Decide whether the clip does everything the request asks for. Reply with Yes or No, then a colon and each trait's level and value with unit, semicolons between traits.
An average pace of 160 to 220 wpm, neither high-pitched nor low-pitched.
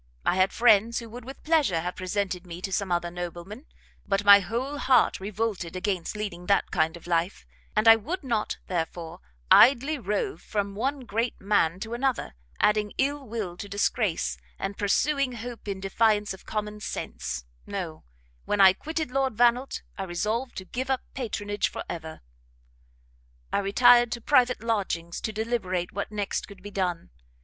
No: average, 170 wpm; high, 210 Hz